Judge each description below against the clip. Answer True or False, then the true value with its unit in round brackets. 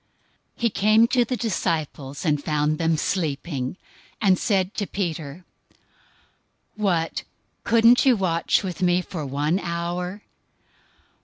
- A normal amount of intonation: True (4.6 semitones)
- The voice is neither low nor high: True (175 Hz)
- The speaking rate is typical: False (125 wpm)